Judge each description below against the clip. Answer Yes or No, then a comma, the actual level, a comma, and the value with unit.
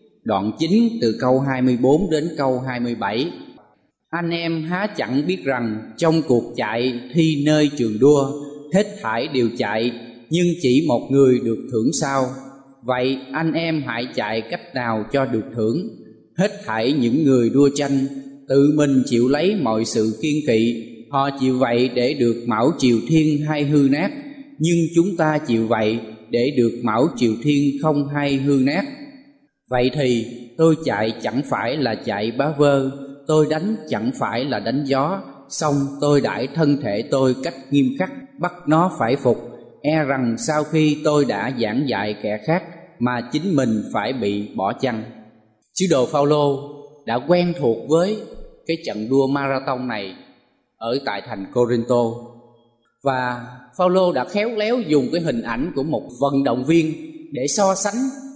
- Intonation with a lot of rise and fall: No, average, 4.5 semitones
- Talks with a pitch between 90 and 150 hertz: Yes, medium, 140 Hz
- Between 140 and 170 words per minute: Yes, slow, 165 wpm